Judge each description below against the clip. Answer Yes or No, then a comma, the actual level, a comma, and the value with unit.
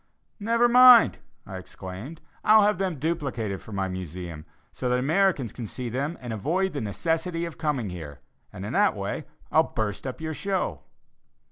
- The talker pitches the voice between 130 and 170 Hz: Yes, low, 135 Hz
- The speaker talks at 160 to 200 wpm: Yes, average, 170 wpm